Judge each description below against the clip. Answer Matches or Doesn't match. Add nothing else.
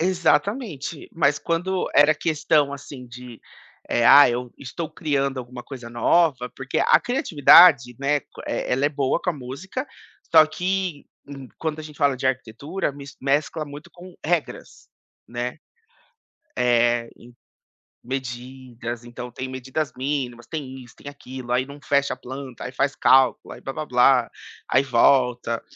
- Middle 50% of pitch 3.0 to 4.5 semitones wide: Matches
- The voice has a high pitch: Doesn't match